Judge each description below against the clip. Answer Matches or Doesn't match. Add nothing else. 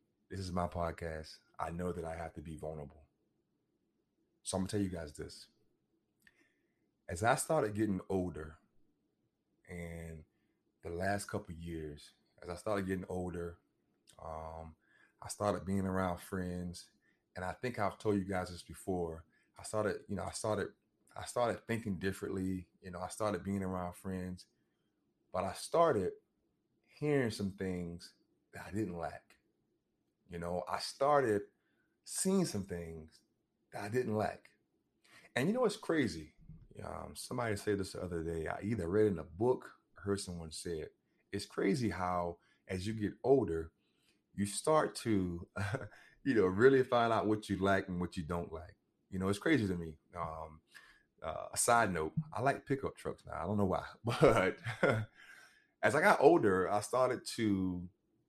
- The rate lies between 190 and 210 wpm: Doesn't match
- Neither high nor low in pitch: Doesn't match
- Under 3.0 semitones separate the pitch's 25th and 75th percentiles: Doesn't match